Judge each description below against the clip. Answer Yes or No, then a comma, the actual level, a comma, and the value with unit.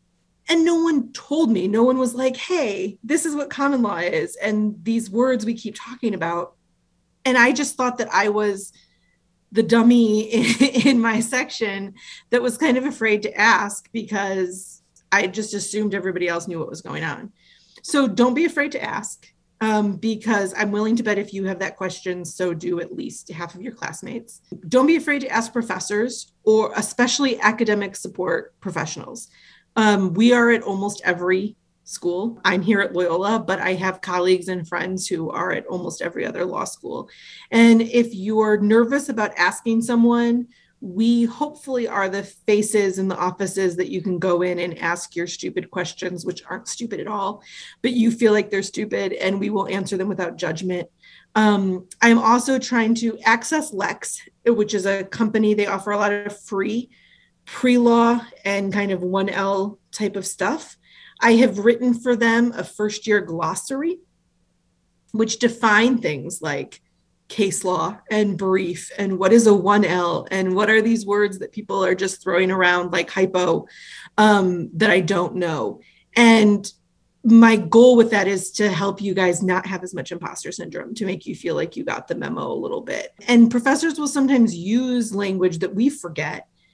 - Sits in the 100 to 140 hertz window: No, high, 210 Hz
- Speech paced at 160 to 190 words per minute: Yes, average, 180 wpm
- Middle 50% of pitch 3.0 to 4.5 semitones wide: Yes, average, 3.8 semitones